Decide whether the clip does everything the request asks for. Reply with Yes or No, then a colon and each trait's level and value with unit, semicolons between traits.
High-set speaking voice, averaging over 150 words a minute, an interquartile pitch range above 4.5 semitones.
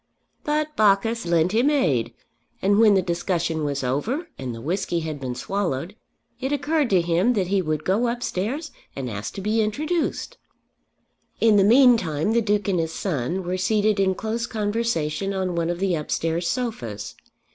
Yes: high, 195 Hz; average, 170 wpm; wide, 5.6 semitones